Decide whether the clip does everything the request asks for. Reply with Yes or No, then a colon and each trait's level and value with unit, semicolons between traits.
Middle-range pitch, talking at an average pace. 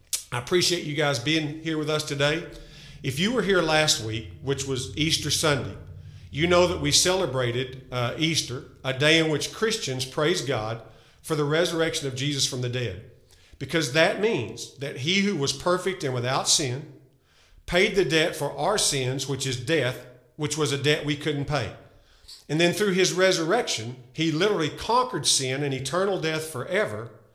Yes: medium, 145 Hz; average, 180 wpm